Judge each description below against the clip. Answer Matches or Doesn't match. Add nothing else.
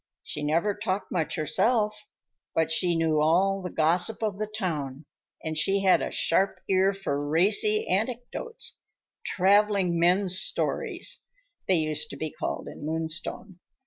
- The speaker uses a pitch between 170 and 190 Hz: Matches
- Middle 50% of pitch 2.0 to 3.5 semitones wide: Doesn't match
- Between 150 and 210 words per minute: Doesn't match